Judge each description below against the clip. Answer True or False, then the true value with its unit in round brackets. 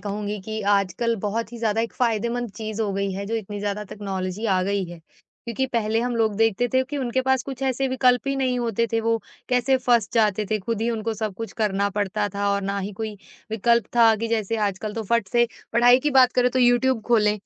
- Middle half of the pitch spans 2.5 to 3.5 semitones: True (2.8 semitones)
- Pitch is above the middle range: True (225 Hz)